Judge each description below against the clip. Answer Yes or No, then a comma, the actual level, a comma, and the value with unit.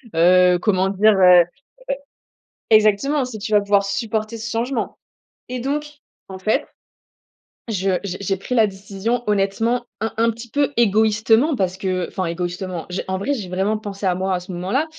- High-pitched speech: Yes, high, 205 Hz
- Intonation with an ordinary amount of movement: Yes, average, 3.4 semitones